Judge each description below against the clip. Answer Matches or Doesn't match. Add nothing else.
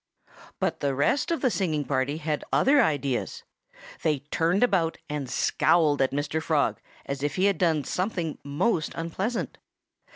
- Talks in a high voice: Doesn't match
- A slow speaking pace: Doesn't match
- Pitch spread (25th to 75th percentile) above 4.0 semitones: Matches